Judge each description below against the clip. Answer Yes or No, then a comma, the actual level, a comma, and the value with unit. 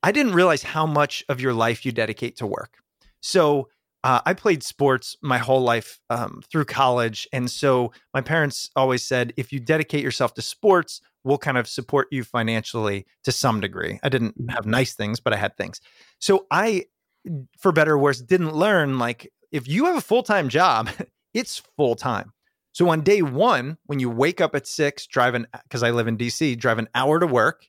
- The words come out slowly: No, average, 200 wpm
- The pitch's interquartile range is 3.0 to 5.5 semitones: Yes, average, 4.3 semitones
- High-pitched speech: No, low, 135 Hz